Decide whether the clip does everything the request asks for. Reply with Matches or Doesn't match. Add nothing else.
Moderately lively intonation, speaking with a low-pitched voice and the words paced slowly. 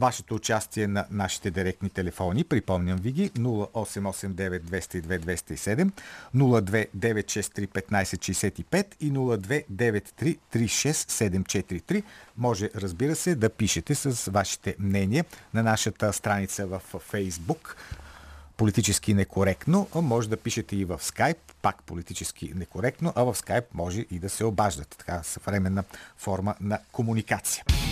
Matches